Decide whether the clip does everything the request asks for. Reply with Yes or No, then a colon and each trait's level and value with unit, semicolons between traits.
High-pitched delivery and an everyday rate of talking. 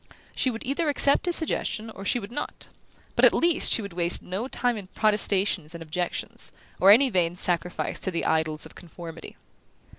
Yes: high, 195 Hz; average, 185 wpm